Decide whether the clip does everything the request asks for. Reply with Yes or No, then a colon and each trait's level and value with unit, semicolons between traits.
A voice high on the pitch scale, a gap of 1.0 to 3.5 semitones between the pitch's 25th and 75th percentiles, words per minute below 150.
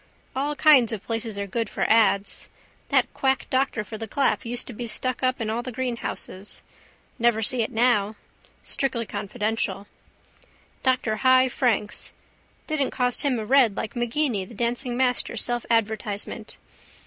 No: high, 235 Hz; average, 3.0 semitones; average, 155 wpm